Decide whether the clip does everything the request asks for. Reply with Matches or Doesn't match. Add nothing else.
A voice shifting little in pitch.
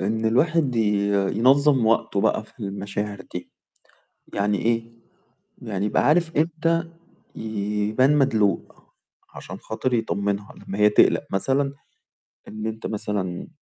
Doesn't match